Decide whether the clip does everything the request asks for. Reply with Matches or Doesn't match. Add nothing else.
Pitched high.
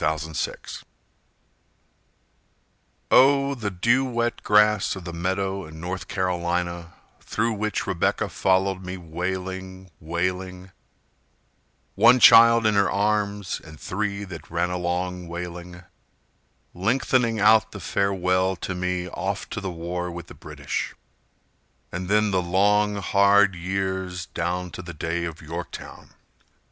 Doesn't match